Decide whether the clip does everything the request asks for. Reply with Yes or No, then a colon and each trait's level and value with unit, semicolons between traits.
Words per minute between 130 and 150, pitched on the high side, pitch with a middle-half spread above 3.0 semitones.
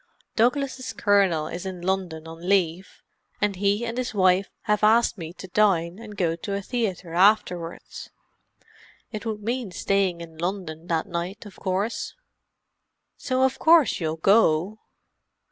Yes: average, 145 wpm; high, 195 Hz; average, 4.1 semitones